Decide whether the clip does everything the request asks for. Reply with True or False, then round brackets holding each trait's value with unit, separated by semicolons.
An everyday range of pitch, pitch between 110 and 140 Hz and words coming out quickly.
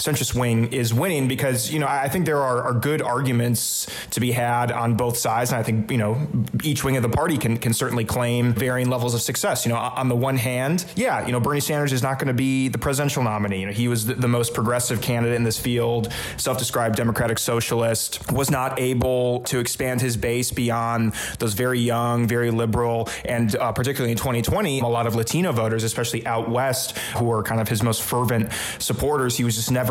False (1.9 semitones; 120 Hz; 220 wpm)